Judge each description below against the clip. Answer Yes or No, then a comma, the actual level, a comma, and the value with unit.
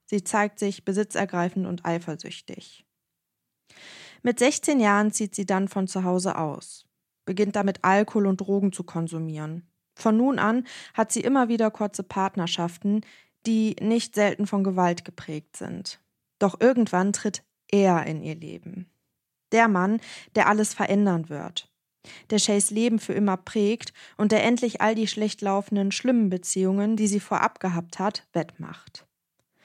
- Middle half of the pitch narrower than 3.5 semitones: Yes, average, 2.9 semitones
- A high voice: Yes, high, 200 Hz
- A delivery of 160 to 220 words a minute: No, average, 150 wpm